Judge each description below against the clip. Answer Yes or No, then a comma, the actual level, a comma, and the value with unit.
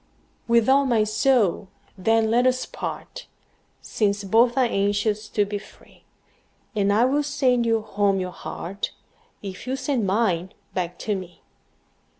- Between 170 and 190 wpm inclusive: No, average, 155 wpm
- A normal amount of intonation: Yes, average, 3.6 semitones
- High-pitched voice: Yes, high, 215 Hz